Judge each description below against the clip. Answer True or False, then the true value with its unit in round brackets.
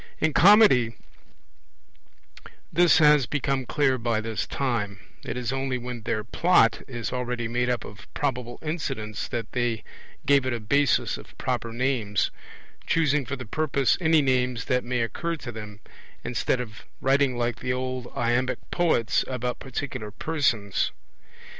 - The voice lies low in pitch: True (125 Hz)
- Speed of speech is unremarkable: True (145 wpm)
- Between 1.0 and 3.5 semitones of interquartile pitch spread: True (3.0 semitones)